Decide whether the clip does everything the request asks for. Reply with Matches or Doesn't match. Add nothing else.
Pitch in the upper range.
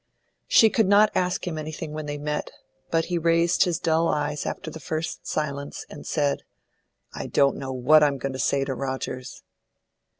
Doesn't match